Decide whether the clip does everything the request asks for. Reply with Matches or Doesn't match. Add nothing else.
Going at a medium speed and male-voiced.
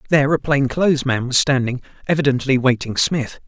Matches